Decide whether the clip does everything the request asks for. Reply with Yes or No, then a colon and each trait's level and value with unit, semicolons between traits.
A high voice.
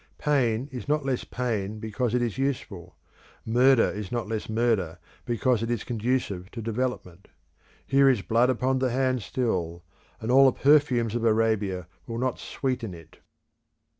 No: low, 120 Hz